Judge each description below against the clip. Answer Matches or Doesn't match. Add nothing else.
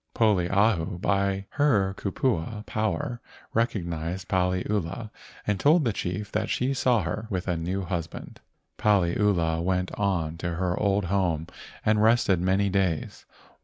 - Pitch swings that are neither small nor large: Matches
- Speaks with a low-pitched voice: Matches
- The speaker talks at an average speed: Doesn't match